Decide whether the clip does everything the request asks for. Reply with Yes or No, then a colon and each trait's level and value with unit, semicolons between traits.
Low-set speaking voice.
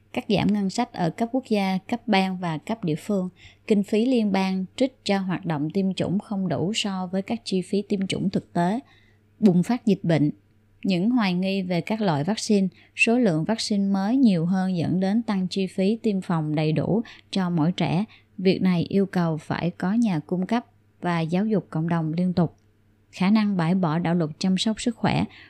No: high, 190 Hz